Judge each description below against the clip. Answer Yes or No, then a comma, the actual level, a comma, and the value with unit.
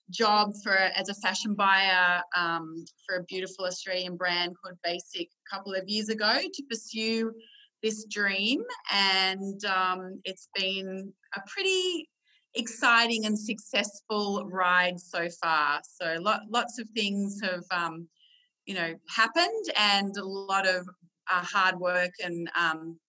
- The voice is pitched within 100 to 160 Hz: No, high, 195 Hz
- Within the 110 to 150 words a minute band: Yes, average, 140 wpm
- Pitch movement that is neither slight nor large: Yes, average, 3.5 semitones